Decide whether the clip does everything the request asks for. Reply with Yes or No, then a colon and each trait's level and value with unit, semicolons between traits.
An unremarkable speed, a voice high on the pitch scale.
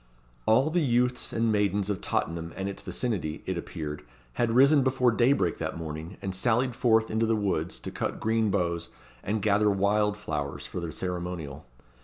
No: average, 175 wpm; low, 105 Hz